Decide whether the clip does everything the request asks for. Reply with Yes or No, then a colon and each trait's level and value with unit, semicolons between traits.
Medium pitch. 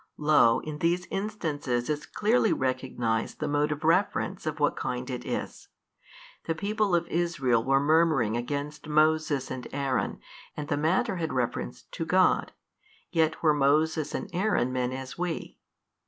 Yes: medium, 150 Hz